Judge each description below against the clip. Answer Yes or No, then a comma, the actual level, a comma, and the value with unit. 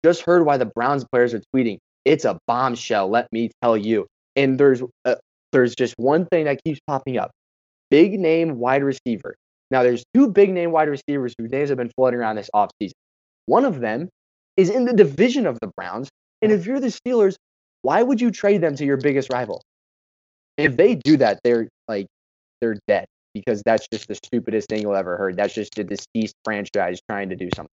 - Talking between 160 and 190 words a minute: No, fast, 205 wpm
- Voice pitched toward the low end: Yes, low, 130 Hz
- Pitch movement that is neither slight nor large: No, wide, 6.9 semitones